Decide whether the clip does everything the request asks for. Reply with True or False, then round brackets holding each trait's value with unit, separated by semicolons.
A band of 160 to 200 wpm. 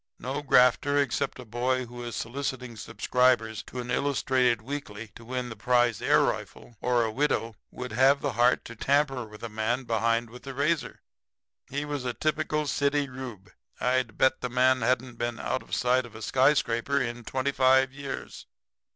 True (180 wpm)